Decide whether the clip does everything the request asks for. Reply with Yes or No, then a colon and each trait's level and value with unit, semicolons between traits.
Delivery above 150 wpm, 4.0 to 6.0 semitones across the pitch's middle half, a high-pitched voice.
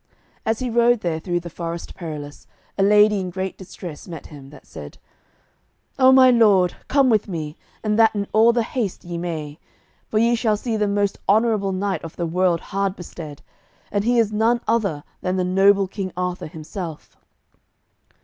Yes: average, 180 wpm; average, 4.3 semitones; high, 195 Hz